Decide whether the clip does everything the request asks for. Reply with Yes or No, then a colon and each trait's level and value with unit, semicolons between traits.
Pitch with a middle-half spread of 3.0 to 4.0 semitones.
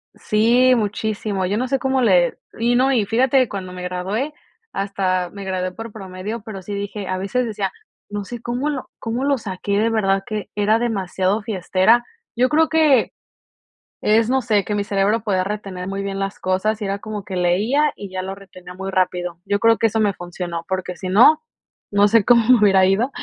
Yes: average, 3.4 semitones